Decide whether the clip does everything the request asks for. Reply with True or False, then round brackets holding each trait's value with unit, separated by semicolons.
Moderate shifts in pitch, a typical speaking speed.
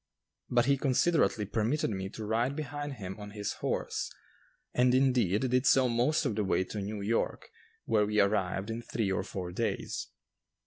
True (4.0 semitones; 175 wpm)